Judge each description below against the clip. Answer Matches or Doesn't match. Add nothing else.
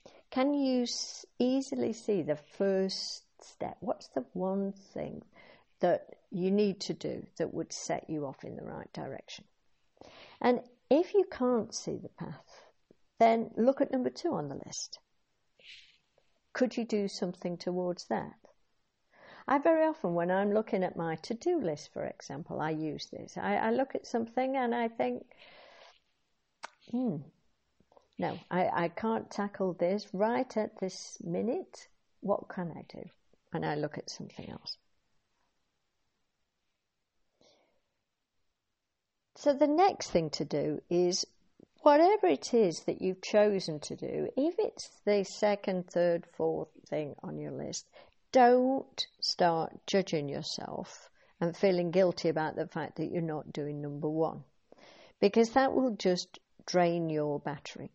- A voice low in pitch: Doesn't match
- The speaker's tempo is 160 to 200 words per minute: Doesn't match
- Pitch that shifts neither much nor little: Doesn't match